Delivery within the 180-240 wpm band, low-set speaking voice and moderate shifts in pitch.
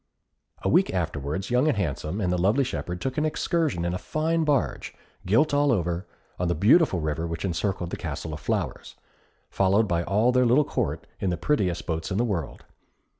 No: average, 195 wpm; very low, 95 Hz; wide, 7.1 semitones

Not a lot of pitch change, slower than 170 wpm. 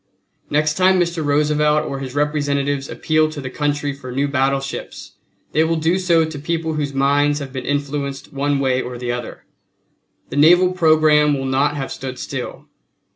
No: narrow, 2.2 semitones; average, 175 wpm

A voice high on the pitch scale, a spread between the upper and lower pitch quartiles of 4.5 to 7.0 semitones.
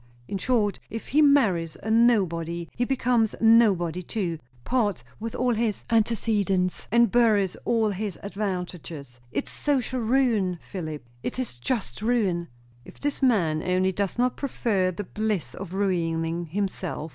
Yes: high, 205 Hz; average, 4.9 semitones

